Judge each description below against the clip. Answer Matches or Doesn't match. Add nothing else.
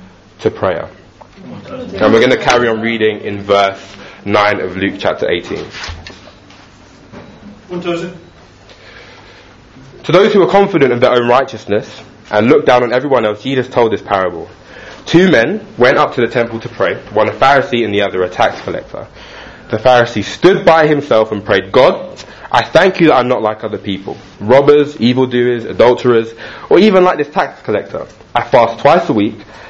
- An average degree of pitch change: Matches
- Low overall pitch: Matches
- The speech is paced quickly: Doesn't match